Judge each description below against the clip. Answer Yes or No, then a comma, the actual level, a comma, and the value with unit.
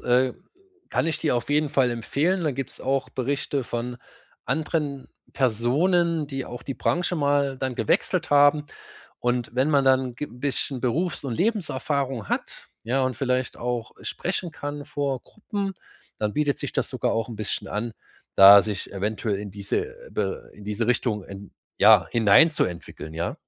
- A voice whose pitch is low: Yes, low, 130 Hz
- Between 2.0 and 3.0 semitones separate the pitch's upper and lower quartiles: No, average, 4.2 semitones